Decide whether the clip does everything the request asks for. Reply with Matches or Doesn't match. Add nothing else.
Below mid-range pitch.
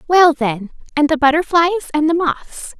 Doesn't match